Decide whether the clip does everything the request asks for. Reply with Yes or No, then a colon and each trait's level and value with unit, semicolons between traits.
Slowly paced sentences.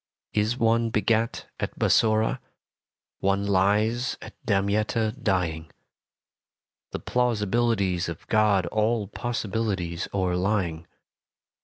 Yes: slow, 90 wpm